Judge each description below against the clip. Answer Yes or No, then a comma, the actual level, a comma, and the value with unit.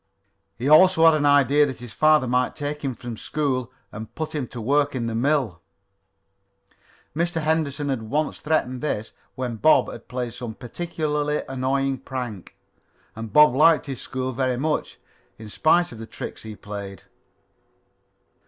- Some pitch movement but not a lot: Yes, average, 3.9 semitones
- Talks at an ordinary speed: Yes, average, 160 wpm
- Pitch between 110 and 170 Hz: Yes, low, 135 Hz